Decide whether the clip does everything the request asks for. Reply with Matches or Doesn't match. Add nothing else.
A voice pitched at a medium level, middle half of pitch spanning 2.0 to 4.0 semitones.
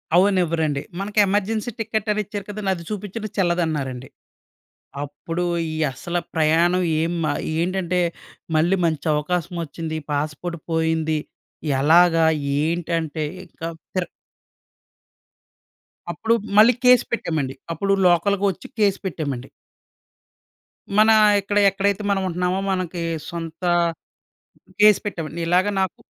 Matches